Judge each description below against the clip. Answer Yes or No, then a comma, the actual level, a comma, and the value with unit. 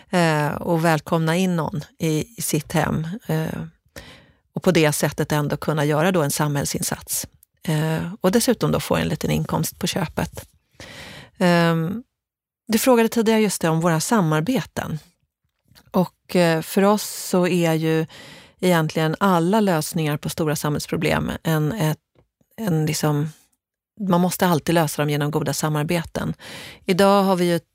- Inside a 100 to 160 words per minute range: Yes, average, 130 wpm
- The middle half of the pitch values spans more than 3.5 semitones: No, average, 3.1 semitones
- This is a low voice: No, medium, 165 Hz